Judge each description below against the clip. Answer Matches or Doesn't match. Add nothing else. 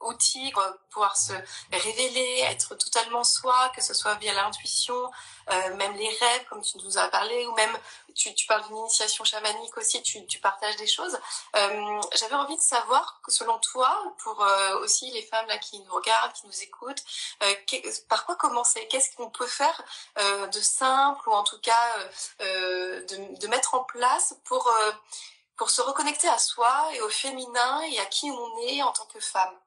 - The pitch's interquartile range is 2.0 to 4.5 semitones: Doesn't match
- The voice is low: Doesn't match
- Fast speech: Doesn't match